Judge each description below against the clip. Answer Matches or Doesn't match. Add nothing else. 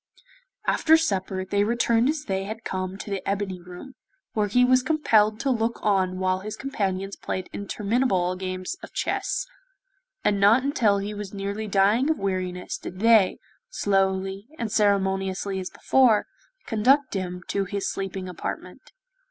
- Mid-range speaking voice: Doesn't match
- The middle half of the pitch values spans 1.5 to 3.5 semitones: Matches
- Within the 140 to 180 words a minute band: Matches